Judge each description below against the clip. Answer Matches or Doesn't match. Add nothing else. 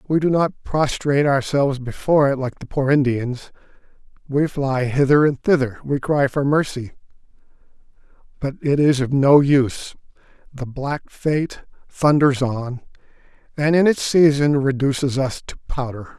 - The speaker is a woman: Doesn't match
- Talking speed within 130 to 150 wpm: Matches